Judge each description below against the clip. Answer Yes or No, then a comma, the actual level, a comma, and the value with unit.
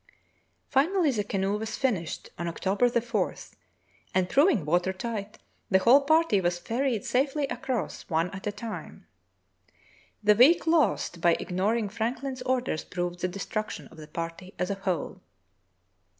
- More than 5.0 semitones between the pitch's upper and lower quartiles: Yes, wide, 5.6 semitones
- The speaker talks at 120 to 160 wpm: Yes, average, 150 wpm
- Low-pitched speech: No, high, 210 Hz